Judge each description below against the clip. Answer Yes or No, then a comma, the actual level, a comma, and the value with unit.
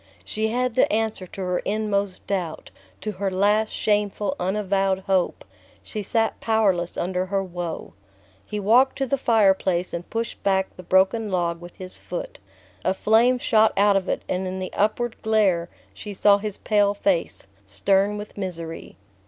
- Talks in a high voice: Yes, high, 200 Hz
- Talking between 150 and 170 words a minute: Yes, average, 165 wpm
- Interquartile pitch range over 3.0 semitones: No, average, 2.7 semitones